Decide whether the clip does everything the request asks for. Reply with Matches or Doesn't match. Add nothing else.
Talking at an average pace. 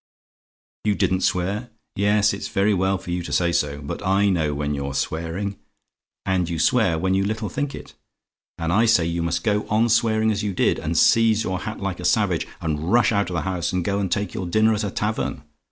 Doesn't match